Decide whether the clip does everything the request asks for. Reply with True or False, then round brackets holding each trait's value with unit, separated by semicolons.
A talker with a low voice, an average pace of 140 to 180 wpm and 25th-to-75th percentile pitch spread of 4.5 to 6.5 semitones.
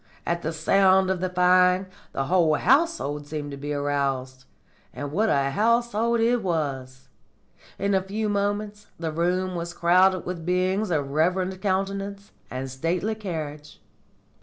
False (180 Hz; 145 wpm; 5.1 semitones)